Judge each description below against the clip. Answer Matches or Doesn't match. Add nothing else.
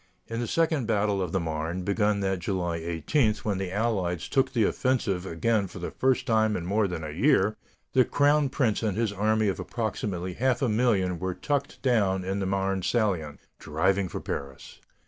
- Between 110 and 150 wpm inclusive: Doesn't match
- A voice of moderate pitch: Doesn't match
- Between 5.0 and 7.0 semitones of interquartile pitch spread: Doesn't match